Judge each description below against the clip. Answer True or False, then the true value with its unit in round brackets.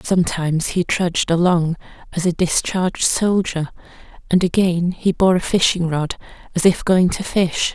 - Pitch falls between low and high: True (175 Hz)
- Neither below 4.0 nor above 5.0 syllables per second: True (4.7 syllables/s)